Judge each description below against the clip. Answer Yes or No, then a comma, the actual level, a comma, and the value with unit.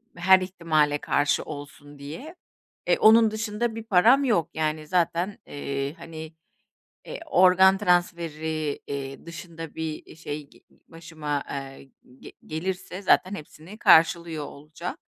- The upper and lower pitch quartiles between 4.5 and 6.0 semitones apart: No, average, 3.8 semitones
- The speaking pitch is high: No, medium, 165 Hz